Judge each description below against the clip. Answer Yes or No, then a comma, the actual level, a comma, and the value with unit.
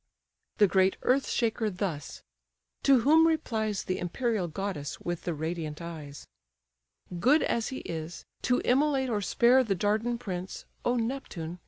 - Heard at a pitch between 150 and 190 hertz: No, high, 205 Hz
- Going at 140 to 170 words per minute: Yes, average, 145 wpm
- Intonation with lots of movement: Yes, wide, 6.2 semitones